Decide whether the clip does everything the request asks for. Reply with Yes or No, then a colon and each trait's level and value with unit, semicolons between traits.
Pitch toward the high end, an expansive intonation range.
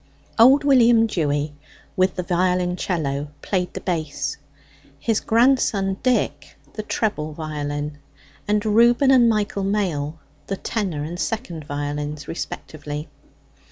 No: medium, 180 Hz; wide, 6.5 semitones